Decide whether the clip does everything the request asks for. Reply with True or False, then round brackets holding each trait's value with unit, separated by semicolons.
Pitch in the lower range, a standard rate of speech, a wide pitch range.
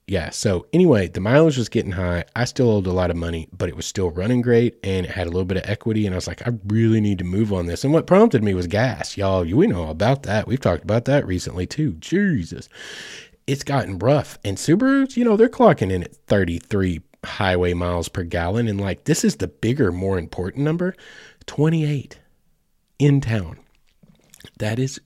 False (105 Hz; 210 wpm; 6.8 semitones)